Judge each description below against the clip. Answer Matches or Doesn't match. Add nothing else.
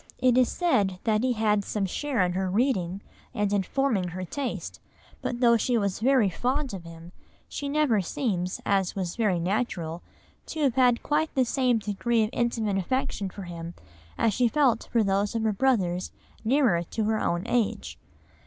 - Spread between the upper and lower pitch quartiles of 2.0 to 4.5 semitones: Doesn't match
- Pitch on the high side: Matches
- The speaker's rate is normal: Matches